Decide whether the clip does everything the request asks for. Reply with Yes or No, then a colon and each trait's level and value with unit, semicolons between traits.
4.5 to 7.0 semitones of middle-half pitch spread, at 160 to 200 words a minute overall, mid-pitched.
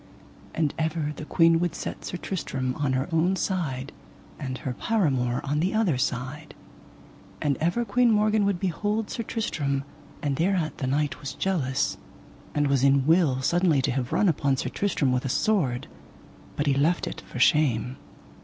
Yes: average, 5.2 semitones; average, 170 wpm; medium, 150 Hz